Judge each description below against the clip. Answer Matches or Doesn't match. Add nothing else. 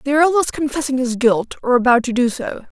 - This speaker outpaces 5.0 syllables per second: Matches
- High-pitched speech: Matches